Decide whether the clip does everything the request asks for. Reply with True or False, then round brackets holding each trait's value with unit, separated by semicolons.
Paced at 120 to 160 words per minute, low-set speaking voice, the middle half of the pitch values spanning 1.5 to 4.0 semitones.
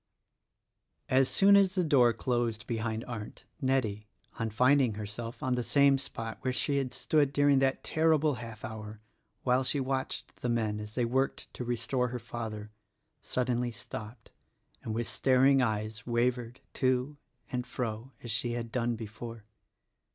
True (155 wpm; 120 Hz; 2.9 semitones)